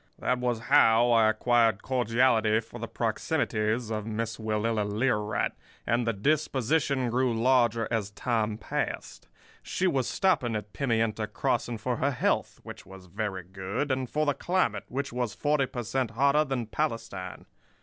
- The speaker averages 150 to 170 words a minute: Yes, average, 155 wpm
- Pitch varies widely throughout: No, average, 3.3 semitones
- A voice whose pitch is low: Yes, low, 115 Hz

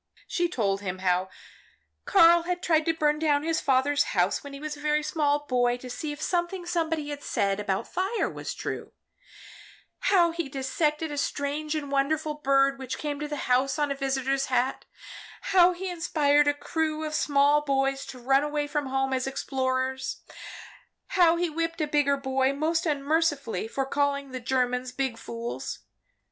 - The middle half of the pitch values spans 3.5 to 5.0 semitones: No, average, 2.8 semitones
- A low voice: No, very high, 285 Hz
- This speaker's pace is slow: No, average, 175 wpm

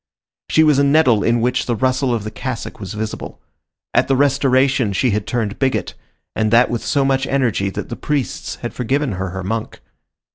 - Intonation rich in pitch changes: No, average, 3.9 semitones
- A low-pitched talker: Yes, low, 125 Hz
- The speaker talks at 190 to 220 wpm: Yes, average, 195 wpm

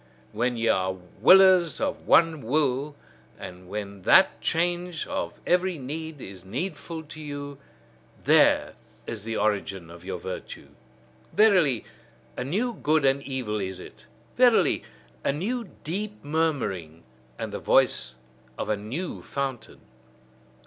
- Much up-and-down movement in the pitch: Yes, wide, 8.2 semitones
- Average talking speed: No, slow, 130 wpm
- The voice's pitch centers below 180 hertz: Yes, medium, 140 Hz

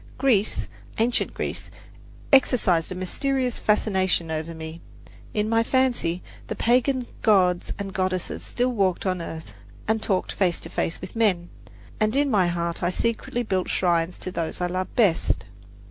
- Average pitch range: Yes, average, 4.7 semitones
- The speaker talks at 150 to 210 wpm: Yes, average, 155 wpm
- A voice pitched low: No, high, 190 Hz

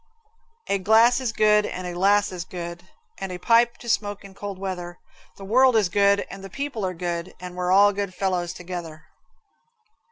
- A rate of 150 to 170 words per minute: No, average, 190 wpm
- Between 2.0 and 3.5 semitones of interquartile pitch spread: Yes, average, 2.8 semitones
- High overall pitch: Yes, high, 195 Hz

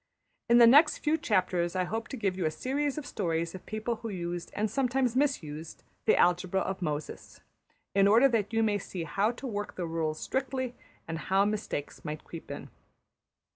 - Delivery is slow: No, average, 195 wpm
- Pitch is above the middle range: Yes, high, 205 Hz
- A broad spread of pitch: Yes, wide, 5.7 semitones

